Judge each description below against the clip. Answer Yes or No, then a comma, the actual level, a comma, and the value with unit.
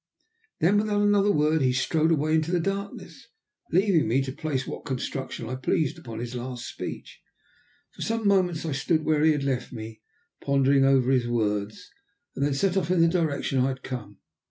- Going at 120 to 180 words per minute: No, average, 190 wpm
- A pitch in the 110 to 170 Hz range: Yes, medium, 140 Hz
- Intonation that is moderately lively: Yes, average, 4.7 semitones